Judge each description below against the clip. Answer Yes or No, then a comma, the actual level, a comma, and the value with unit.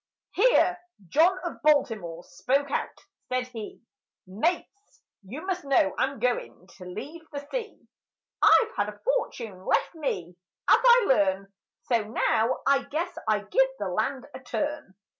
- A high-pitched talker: Yes, very high, 265 Hz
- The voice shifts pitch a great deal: Yes, wide, 7.8 semitones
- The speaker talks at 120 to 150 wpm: Yes, average, 145 wpm